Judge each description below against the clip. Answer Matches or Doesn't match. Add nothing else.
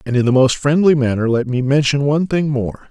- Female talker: Doesn't match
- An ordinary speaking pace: Doesn't match